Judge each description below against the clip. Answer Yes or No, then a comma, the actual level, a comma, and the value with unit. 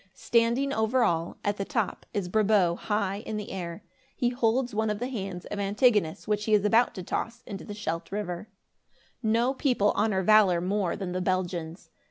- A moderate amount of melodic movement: Yes, average, 3.4 semitones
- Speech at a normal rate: Yes, average, 185 wpm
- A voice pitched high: Yes, high, 210 Hz